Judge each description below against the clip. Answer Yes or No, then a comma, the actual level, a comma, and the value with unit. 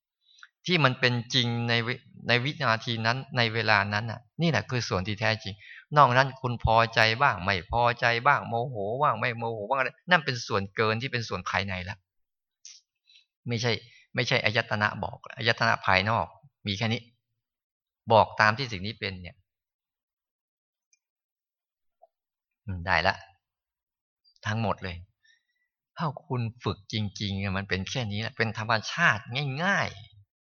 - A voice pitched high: No, low, 115 Hz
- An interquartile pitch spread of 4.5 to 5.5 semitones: No, average, 3.8 semitones